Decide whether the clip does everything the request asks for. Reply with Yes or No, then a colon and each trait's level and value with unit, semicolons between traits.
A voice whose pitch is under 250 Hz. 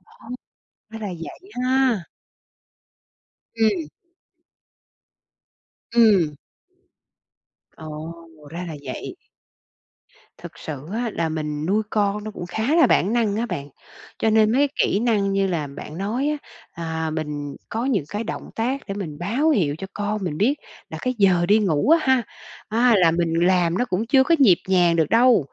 Yes: high, 200 Hz